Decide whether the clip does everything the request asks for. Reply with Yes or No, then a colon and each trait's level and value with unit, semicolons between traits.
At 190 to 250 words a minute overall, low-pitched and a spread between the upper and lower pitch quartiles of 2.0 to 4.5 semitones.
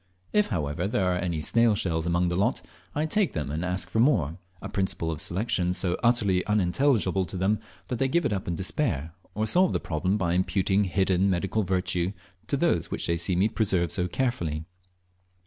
Yes: average, 200 wpm; very low, 95 Hz; average, 3.7 semitones